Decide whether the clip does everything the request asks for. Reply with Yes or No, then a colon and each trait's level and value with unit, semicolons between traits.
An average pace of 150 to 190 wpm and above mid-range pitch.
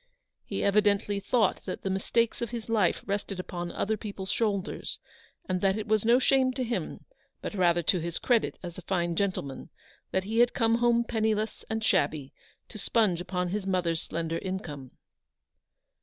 Yes: average, 170 wpm; high, 200 Hz